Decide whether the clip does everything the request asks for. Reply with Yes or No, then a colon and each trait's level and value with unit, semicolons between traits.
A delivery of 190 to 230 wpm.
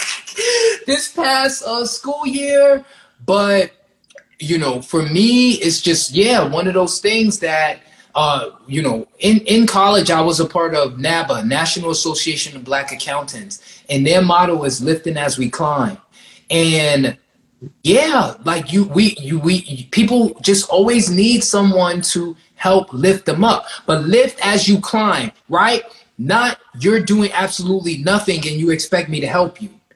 No: average, 155 wpm